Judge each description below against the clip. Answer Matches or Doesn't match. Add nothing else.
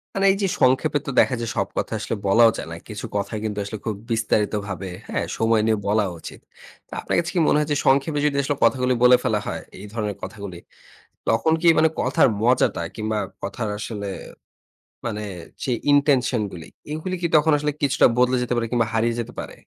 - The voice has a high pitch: Doesn't match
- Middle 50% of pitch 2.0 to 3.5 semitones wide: Doesn't match